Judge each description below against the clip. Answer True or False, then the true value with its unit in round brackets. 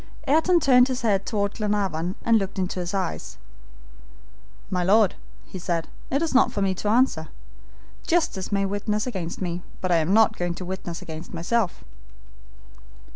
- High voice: True (195 Hz)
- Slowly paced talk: False (165 wpm)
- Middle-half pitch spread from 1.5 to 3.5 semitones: False (4.0 semitones)